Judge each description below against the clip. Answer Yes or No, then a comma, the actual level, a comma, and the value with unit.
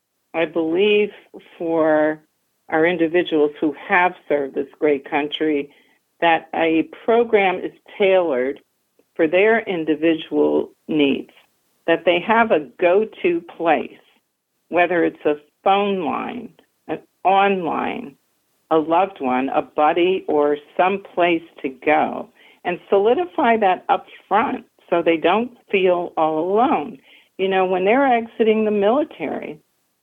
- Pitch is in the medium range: Yes, medium, 175 Hz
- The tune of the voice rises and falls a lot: No, average, 4.1 semitones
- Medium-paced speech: No, slow, 120 wpm